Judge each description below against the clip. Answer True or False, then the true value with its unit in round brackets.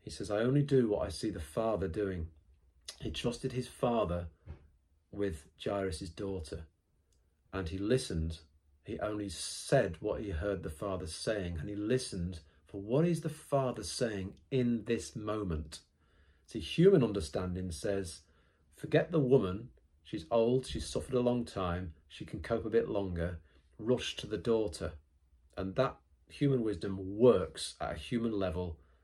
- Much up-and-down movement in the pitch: True (5.7 semitones)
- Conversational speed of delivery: True (155 wpm)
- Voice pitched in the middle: False (95 Hz)